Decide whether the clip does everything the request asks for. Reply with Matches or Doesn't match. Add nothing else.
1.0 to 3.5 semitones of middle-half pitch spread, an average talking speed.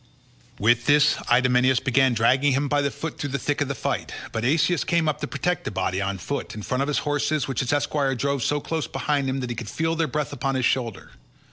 Doesn't match